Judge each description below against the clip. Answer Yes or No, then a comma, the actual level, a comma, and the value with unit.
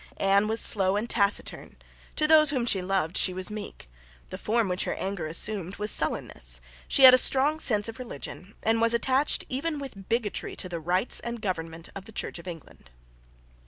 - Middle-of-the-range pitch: No, high, 205 Hz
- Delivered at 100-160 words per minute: No, average, 195 wpm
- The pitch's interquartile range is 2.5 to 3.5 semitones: No, average, 4.4 semitones